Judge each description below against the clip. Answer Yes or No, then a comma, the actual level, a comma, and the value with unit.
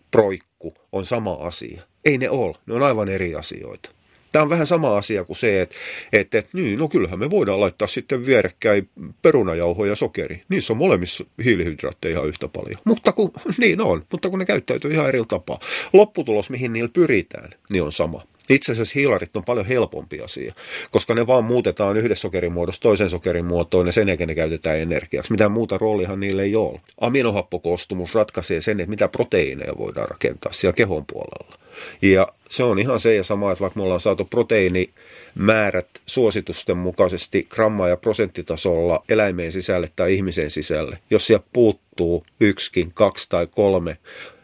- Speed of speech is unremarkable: No, fast, 170 wpm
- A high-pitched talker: No, low, 100 Hz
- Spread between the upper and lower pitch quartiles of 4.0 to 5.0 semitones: Yes, average, 4.7 semitones